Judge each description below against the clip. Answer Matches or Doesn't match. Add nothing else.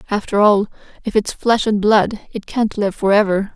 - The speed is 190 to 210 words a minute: Matches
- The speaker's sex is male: Doesn't match